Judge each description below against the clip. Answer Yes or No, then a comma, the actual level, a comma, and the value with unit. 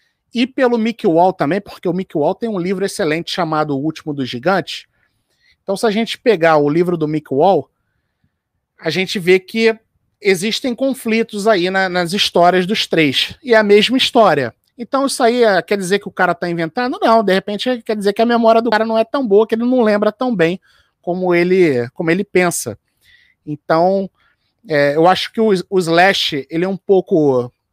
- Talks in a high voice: Yes, high, 195 Hz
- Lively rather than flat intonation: No, average, 4.7 semitones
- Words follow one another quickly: Yes, fast, 195 wpm